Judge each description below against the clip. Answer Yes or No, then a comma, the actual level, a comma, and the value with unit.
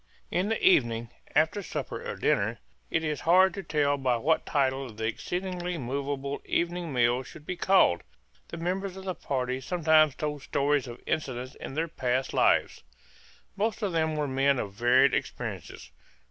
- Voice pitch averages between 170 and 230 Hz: No, medium, 145 Hz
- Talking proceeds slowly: No, average, 165 wpm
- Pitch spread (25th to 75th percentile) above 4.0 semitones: Yes, average, 4.9 semitones